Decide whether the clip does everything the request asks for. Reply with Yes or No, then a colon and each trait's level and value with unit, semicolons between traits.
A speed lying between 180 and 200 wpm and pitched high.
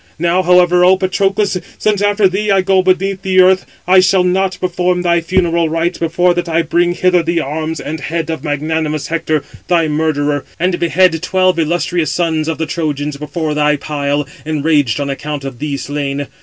No: average, 185 wpm; medium, 170 Hz